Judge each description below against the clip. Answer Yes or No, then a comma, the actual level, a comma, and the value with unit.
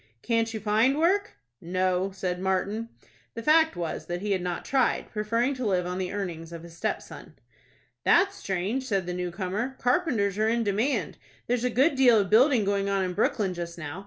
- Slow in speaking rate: No, average, 195 wpm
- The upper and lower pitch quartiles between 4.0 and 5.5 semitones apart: Yes, average, 5.1 semitones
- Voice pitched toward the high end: Yes, high, 205 Hz